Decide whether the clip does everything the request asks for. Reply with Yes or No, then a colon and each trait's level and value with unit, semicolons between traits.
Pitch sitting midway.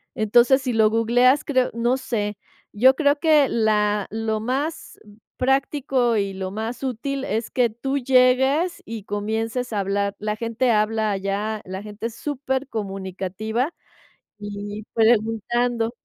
No: high, 225 Hz